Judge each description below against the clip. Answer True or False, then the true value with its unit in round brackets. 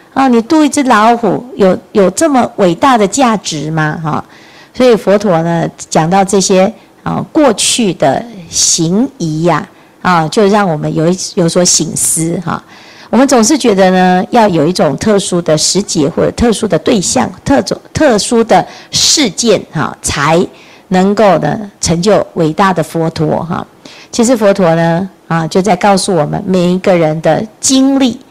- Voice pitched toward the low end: False (190 Hz)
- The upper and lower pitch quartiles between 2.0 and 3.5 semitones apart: False (5.3 semitones)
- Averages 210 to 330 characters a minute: True (250 characters per minute)